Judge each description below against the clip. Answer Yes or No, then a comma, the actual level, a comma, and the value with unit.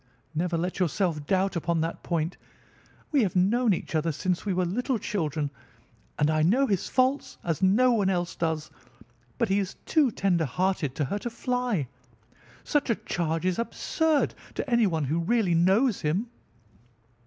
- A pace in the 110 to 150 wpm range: No, average, 165 wpm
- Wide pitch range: Yes, wide, 5.8 semitones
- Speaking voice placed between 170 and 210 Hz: Yes, medium, 185 Hz